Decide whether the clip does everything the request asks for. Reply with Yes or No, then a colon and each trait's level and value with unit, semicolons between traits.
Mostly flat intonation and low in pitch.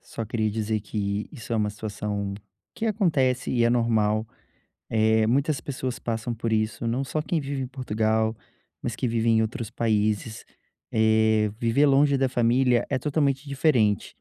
No: average, 3.3 semitones; low, 115 Hz